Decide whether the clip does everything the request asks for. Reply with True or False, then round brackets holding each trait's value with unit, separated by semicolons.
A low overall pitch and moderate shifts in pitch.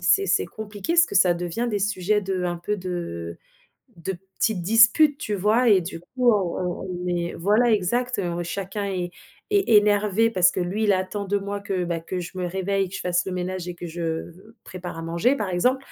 False (190 Hz; 3.1 semitones)